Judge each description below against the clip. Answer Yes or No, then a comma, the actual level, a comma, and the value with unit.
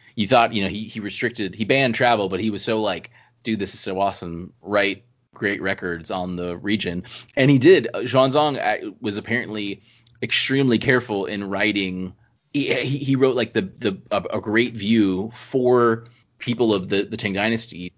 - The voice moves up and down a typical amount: Yes, average, 3.7 semitones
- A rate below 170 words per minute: No, average, 175 wpm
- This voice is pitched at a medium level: No, low, 110 Hz